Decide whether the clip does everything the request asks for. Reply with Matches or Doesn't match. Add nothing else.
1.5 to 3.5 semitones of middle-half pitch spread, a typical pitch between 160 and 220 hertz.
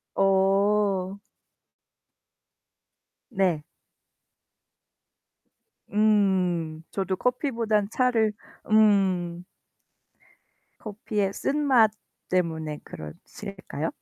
Matches